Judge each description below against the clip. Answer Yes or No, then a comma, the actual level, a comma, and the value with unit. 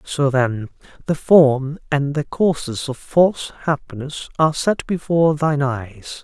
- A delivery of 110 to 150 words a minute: Yes, average, 145 wpm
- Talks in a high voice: No, medium, 145 Hz